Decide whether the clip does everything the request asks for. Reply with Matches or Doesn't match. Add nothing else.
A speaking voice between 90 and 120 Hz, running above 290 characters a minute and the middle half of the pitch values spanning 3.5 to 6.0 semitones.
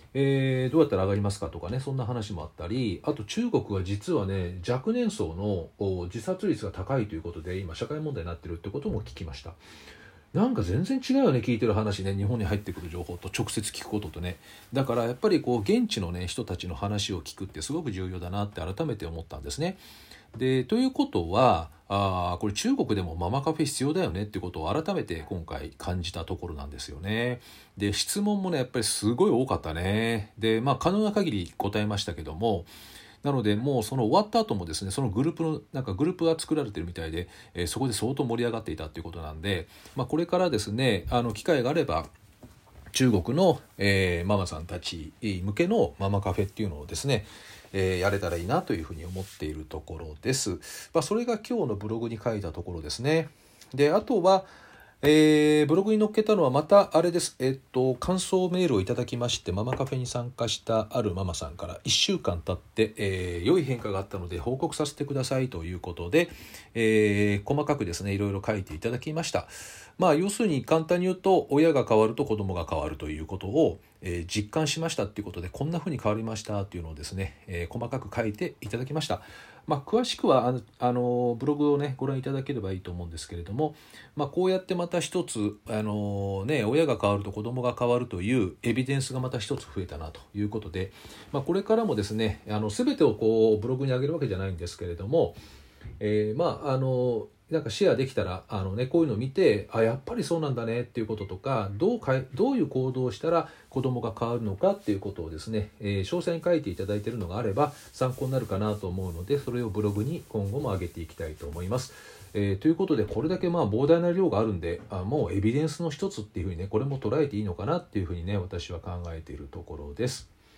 Doesn't match